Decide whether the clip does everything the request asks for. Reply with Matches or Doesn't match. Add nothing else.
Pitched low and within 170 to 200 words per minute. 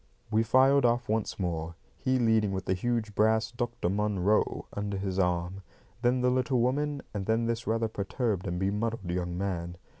Matches